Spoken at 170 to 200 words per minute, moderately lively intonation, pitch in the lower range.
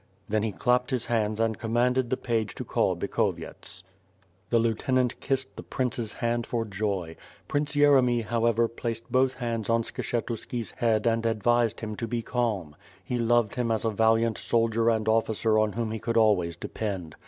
No: average, 175 wpm; narrow, 1.7 semitones; low, 115 Hz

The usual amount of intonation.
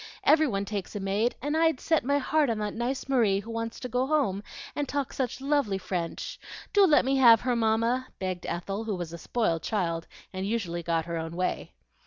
No: wide, 5.9 semitones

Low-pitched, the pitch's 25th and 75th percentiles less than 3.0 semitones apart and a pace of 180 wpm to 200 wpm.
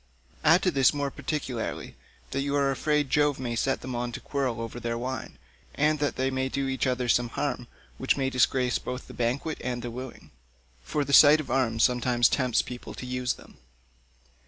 Yes: low, 130 Hz; narrow, 2.5 semitones; average, 190 wpm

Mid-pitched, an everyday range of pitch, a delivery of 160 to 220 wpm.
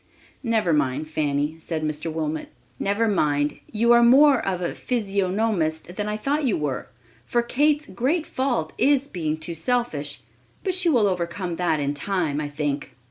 No: medium, 180 Hz; wide, 7.5 semitones; average, 165 wpm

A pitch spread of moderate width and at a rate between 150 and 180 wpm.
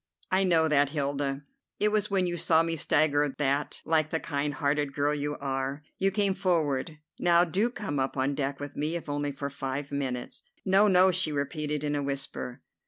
No: average, 3.4 semitones; average, 195 wpm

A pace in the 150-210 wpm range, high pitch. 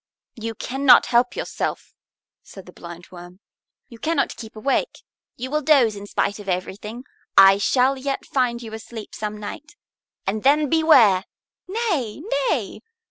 No: average, 140 wpm; high, 230 Hz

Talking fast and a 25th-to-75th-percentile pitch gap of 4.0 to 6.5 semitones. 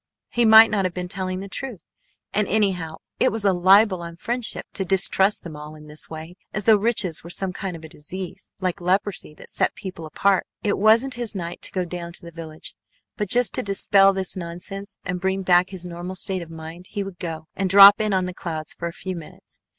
No: fast, 225 wpm; average, 2.7 semitones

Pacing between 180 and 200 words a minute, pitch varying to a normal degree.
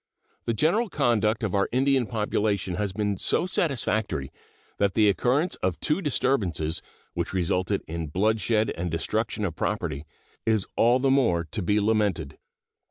No: average, 150 wpm; average, 4.8 semitones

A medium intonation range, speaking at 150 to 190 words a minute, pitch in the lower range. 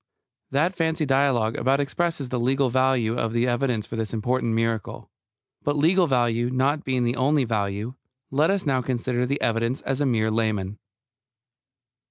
Yes: average, 3.3 semitones; average, 160 wpm; low, 125 Hz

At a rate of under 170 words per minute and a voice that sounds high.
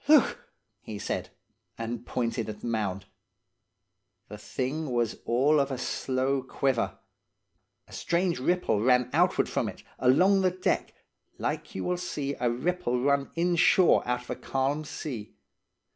No: average, 145 wpm; low, 130 Hz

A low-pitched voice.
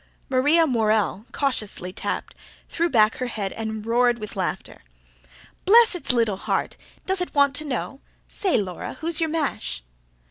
No: very high, 250 Hz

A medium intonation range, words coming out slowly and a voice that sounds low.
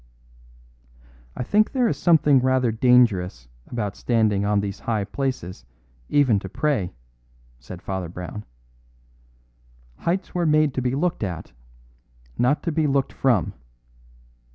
No: wide, 6.7 semitones; slow, 130 wpm; low, 120 Hz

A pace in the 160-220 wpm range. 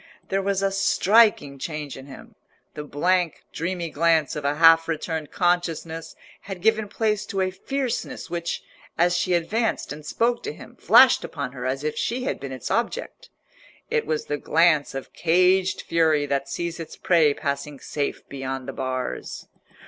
Yes: average, 170 wpm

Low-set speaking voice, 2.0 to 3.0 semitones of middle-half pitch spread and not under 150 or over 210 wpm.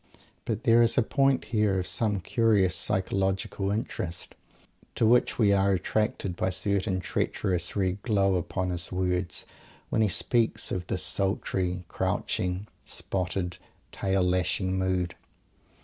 No: very low, 95 Hz; average, 2.7 semitones; slow, 135 wpm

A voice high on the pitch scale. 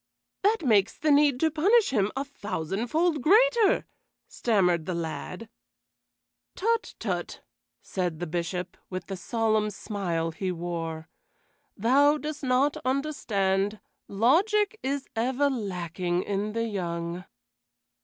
Yes: high, 215 Hz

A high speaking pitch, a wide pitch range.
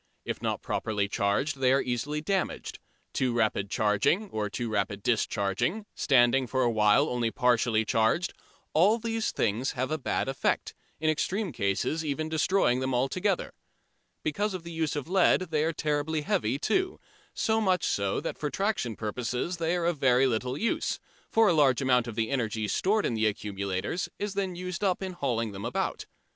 No: low, 135 Hz; wide, 7.4 semitones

